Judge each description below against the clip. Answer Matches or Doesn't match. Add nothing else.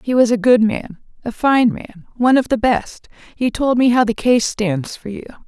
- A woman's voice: Matches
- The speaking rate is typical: Doesn't match